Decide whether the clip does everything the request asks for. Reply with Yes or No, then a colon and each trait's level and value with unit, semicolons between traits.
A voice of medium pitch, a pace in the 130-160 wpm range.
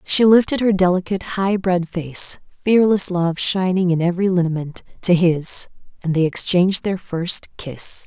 Yes: medium, 180 Hz; average, 155 wpm